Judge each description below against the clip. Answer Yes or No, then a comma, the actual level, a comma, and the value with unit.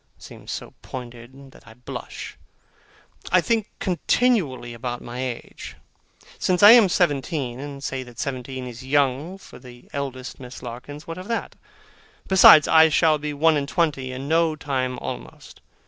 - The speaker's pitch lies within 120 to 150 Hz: Yes, medium, 140 Hz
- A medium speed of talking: Yes, average, 155 wpm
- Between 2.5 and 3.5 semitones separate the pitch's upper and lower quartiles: No, average, 4.3 semitones